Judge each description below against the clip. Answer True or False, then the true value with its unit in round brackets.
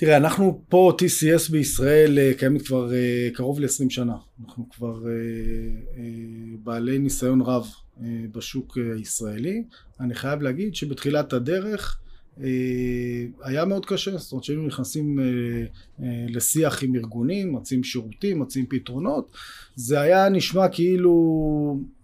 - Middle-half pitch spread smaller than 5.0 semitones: True (4.1 semitones)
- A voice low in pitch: True (130 Hz)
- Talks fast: False (130 wpm)